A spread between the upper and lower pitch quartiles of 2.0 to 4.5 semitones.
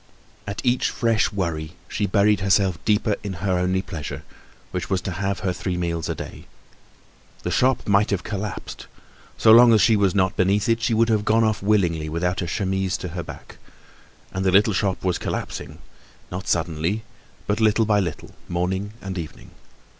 Yes: average, 2.8 semitones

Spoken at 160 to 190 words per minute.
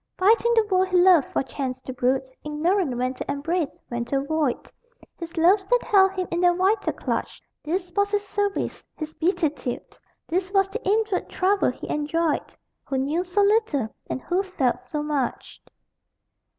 Yes: average, 170 wpm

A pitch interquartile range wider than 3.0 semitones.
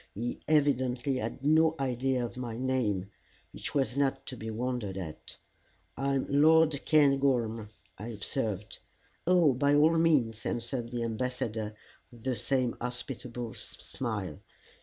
Yes: average, 3.4 semitones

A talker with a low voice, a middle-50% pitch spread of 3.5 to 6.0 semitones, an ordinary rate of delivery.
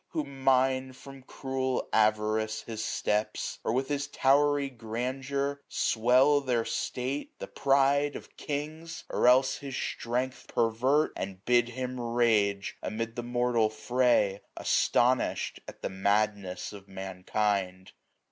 No: low, 125 Hz; average, 3.8 semitones; slow, 130 wpm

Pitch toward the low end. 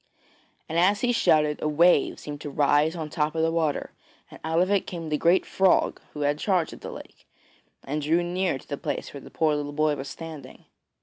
No: medium, 155 Hz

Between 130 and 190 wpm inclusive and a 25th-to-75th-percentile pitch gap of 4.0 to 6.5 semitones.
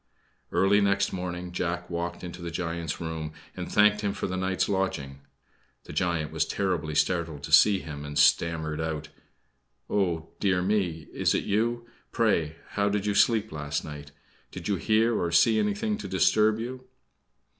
Yes: average, 165 wpm; average, 4.3 semitones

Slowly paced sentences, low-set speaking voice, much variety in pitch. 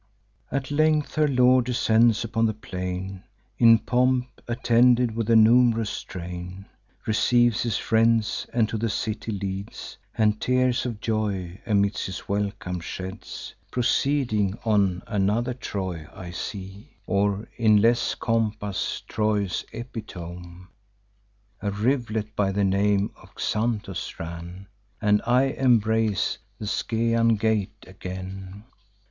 No: slow, 120 wpm; low, 110 Hz; average, 3.3 semitones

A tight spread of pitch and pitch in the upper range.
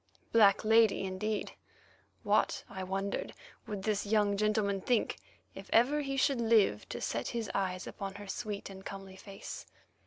Yes: narrow, 2.3 semitones; high, 205 Hz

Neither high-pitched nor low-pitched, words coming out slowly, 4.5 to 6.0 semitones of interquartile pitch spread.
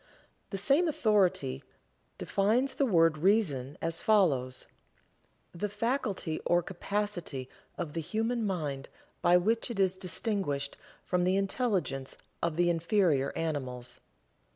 Yes: medium, 180 Hz; slow, 120 wpm; average, 5.3 semitones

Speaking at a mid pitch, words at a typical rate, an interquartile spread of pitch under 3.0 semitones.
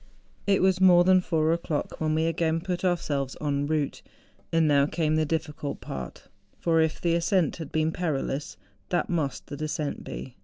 Yes: medium, 160 Hz; average, 180 wpm; narrow, 2.6 semitones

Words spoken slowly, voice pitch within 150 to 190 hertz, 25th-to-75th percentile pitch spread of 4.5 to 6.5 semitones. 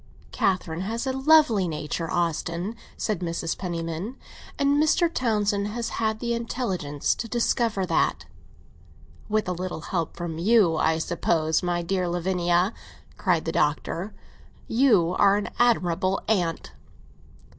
Yes: slow, 130 wpm; medium, 185 Hz; average, 4.9 semitones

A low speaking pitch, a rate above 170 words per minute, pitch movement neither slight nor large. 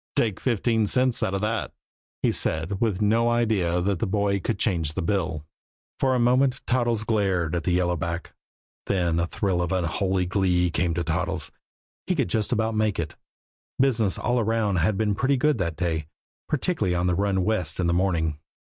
Yes: very low, 95 Hz; average, 190 wpm; average, 4.3 semitones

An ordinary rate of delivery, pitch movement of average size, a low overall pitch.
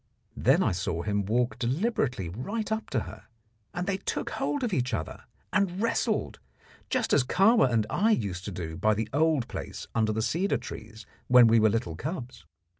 No: average, 190 wpm; wide, 8.9 semitones; low, 120 Hz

